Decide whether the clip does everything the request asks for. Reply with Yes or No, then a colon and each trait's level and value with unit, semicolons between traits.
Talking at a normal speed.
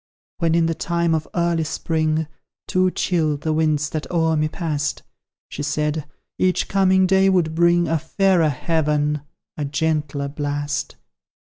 Yes: average, 145 wpm